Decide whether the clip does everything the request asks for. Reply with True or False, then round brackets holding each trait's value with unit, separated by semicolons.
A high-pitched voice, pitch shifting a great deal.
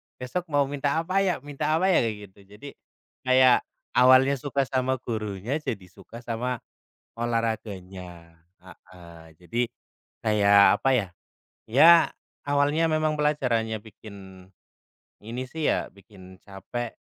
False (120 Hz; 6.0 semitones)